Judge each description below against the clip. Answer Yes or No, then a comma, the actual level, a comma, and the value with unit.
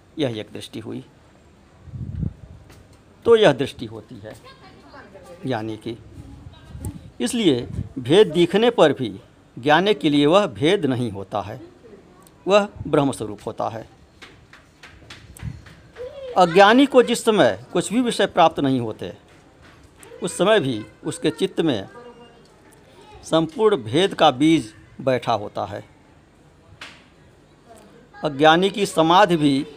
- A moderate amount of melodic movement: No, wide, 8.1 semitones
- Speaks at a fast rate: No, slow, 110 wpm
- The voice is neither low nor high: Yes, medium, 160 Hz